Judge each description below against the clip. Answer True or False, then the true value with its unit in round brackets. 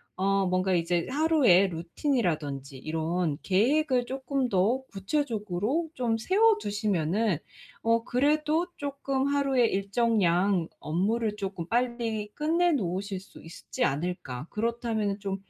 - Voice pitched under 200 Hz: False (210 Hz)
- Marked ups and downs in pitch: True (6.5 semitones)